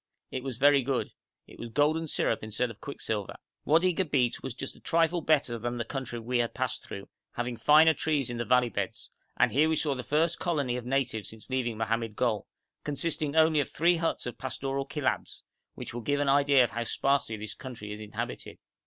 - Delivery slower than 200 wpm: No, fast, 205 wpm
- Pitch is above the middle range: No, low, 130 Hz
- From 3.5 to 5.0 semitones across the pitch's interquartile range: Yes, average, 4.0 semitones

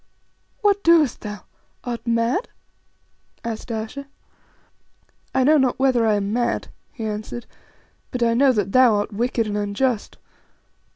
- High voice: Yes, high, 235 Hz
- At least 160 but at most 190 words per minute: No, slow, 135 wpm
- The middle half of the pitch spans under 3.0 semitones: No, average, 3.4 semitones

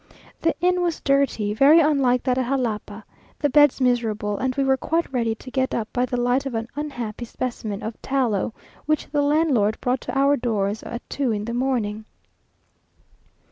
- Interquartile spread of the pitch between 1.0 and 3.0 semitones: No, average, 3.8 semitones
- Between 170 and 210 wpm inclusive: Yes, average, 180 wpm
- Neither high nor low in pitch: No, very high, 250 Hz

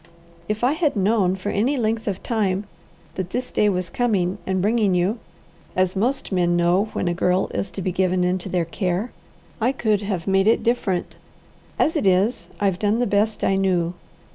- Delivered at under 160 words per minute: No, average, 190 wpm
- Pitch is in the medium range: No, high, 195 Hz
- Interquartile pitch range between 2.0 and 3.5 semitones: Yes, average, 3.2 semitones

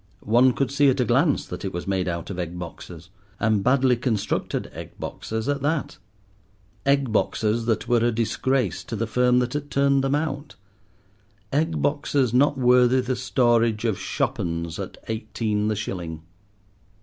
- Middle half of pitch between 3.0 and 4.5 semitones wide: No, average, 5.0 semitones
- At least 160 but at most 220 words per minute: Yes, average, 165 wpm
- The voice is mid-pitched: No, low, 120 Hz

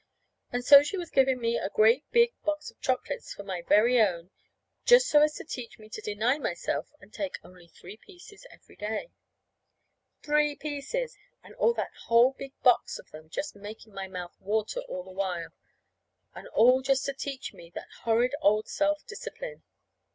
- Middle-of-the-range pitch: No, very high, 250 Hz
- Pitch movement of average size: No, wide, 6.6 semitones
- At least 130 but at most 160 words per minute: No, average, 180 wpm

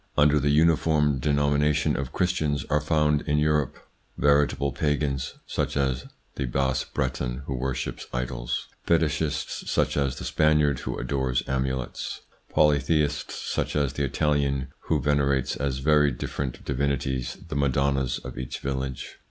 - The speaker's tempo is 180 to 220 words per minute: No, average, 140 wpm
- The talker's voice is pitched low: Yes, very low, 70 Hz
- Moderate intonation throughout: No, narrow, 2.0 semitones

